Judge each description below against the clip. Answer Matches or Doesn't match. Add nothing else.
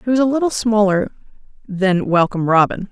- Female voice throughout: Matches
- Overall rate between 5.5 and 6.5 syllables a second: Matches